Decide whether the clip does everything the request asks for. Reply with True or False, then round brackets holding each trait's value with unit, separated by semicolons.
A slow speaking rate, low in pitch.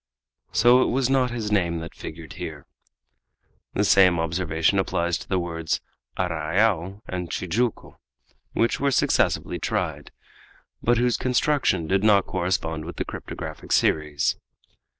True (130 wpm; 95 Hz)